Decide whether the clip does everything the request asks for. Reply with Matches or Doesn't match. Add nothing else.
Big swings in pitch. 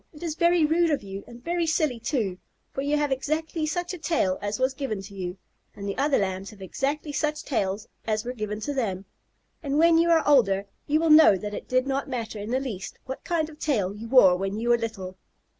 Matches